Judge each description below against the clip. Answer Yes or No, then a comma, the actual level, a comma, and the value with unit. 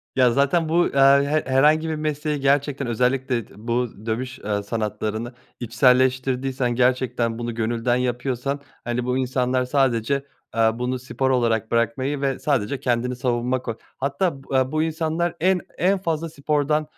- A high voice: No, low, 130 Hz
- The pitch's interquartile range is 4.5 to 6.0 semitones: No, average, 2.9 semitones